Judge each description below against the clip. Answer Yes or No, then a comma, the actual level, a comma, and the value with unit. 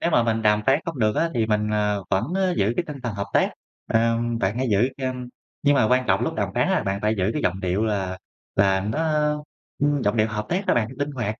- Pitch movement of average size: Yes, average, 3.8 semitones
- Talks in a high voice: No, low, 110 Hz